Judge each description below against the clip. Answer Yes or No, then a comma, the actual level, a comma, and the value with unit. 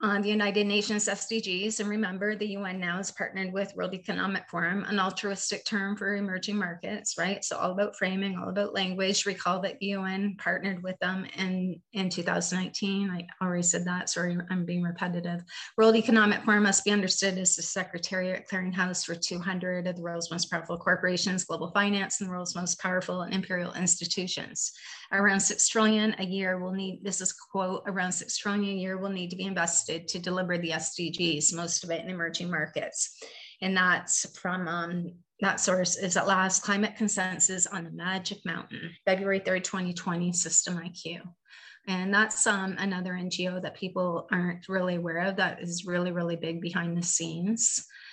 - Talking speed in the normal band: Yes, average, 180 wpm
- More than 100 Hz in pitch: Yes, medium, 185 Hz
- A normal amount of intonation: No, narrow, 2.0 semitones